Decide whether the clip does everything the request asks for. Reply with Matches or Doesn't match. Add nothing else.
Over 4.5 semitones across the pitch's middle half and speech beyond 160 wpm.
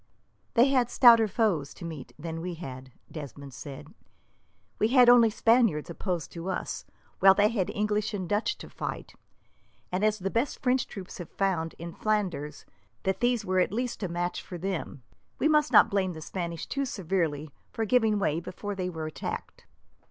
Matches